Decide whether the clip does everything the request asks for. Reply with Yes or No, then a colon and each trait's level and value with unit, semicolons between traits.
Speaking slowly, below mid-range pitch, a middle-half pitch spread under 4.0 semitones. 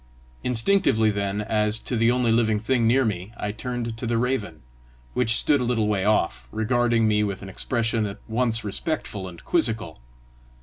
No: average, 175 wpm; low, 110 Hz; narrow, 2.6 semitones